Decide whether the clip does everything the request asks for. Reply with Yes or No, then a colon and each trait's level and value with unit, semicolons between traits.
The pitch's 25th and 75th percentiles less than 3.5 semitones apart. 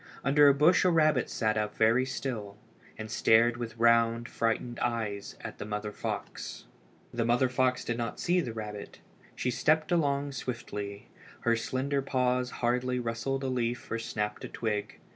Yes: average, 2.7 semitones